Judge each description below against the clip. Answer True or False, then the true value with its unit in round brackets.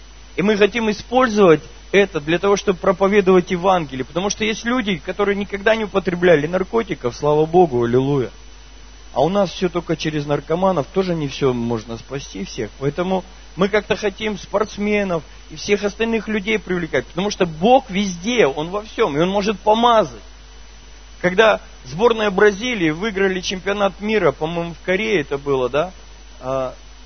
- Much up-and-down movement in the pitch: True (5.8 semitones)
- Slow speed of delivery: False (150 wpm)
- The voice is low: False (185 Hz)